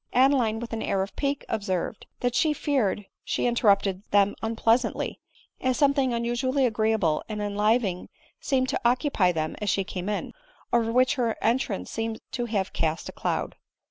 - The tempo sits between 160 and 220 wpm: Yes, average, 170 wpm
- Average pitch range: Yes, average, 3.9 semitones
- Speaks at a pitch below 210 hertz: No, high, 225 Hz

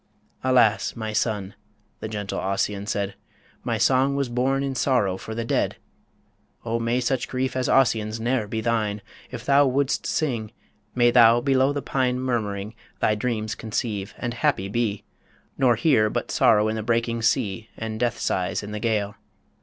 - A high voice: No, low, 115 Hz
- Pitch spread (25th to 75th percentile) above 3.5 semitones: No, average, 3.1 semitones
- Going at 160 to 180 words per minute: Yes, average, 170 wpm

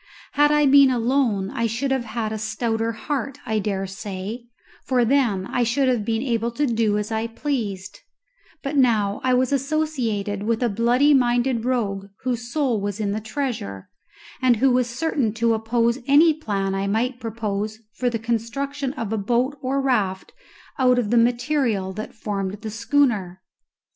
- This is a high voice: Yes, high, 235 Hz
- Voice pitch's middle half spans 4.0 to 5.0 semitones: No, average, 3.5 semitones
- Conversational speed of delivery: Yes, average, 175 wpm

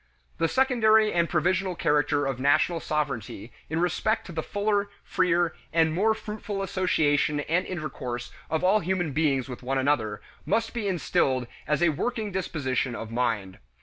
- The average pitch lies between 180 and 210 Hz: No, medium, 160 Hz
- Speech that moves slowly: No, average, 155 wpm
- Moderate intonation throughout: No, wide, 5.7 semitones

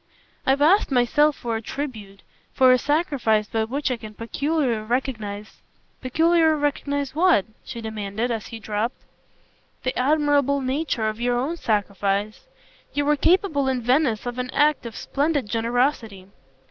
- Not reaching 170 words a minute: Yes, average, 150 wpm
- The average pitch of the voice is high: Yes, very high, 255 Hz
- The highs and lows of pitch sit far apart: No, average, 4.8 semitones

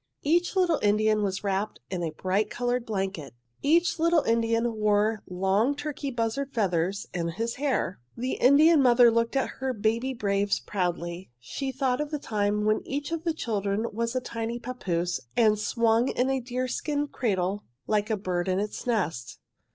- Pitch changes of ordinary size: Yes, average, 4.6 semitones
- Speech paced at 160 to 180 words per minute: Yes, average, 170 wpm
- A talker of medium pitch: No, high, 225 Hz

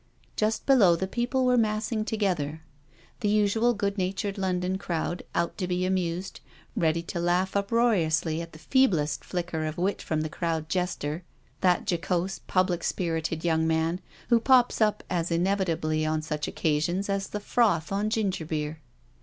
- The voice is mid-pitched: Yes, medium, 180 Hz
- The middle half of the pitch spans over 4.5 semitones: No, average, 3.9 semitones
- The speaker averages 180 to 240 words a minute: No, average, 155 wpm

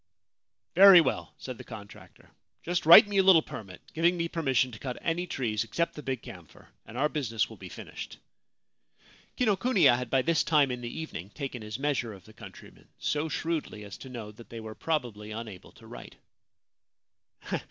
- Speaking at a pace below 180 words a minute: No, average, 195 wpm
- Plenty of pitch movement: Yes, wide, 6.9 semitones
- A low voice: Yes, low, 130 Hz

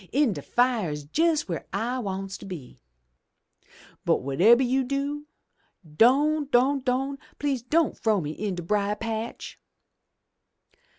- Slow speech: Yes, slow, 130 wpm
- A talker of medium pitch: No, high, 240 Hz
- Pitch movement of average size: No, wide, 5.8 semitones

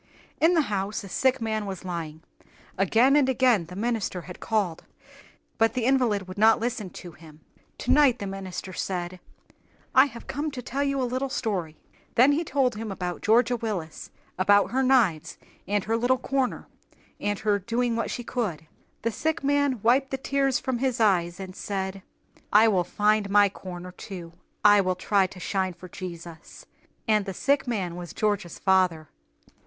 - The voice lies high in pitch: Yes, high, 210 Hz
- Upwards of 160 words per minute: Yes, average, 175 wpm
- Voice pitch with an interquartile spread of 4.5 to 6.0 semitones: Yes, average, 5.2 semitones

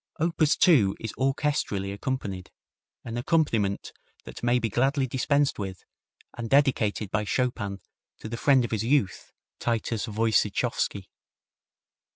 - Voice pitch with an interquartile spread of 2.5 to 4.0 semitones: No, average, 4.7 semitones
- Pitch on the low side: Yes, low, 115 Hz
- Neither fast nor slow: No, slow, 125 wpm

